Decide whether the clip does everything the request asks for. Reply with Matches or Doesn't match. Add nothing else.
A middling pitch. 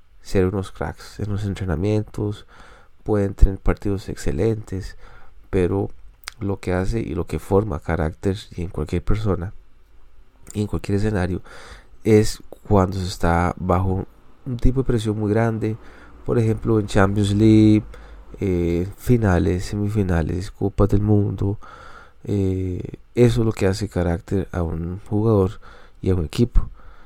Doesn't match